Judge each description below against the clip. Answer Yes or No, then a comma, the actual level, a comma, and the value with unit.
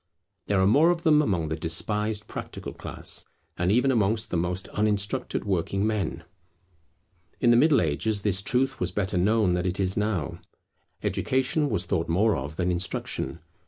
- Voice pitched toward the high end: No, low, 100 Hz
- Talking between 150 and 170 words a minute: Yes, average, 165 wpm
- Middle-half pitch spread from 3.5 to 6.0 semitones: Yes, average, 3.9 semitones